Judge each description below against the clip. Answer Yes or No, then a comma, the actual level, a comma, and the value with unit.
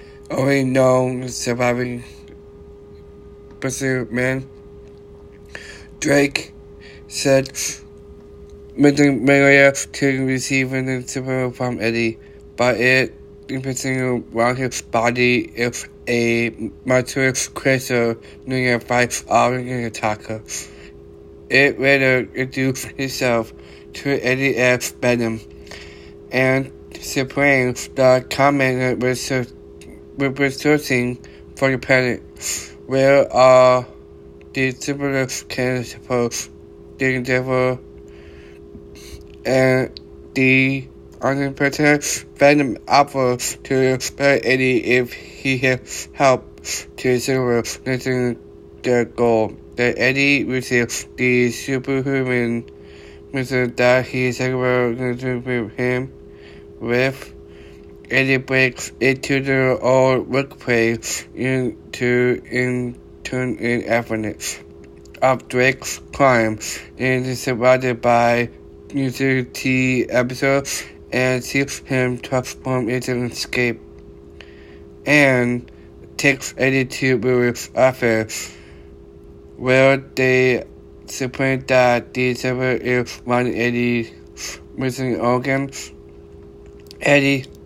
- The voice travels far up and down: Yes, wide, 8.1 semitones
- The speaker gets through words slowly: Yes, slow, 90 wpm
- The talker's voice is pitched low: Yes, low, 125 Hz